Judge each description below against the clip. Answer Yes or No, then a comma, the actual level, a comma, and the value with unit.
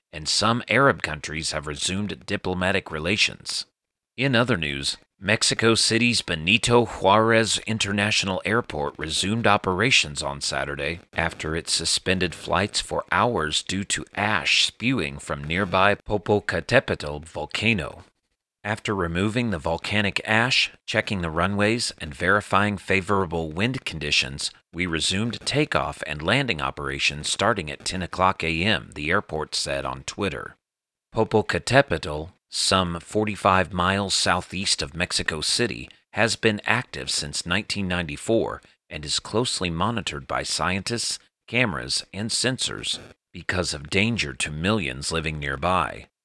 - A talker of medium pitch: No, very low, 95 Hz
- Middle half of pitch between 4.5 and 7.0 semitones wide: Yes, average, 5.0 semitones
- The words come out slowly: Yes, slow, 125 wpm